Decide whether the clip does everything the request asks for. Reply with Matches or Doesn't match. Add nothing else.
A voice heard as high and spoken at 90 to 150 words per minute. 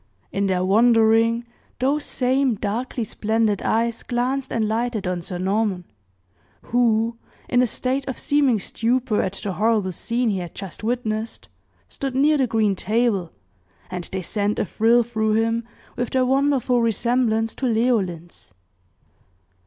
Matches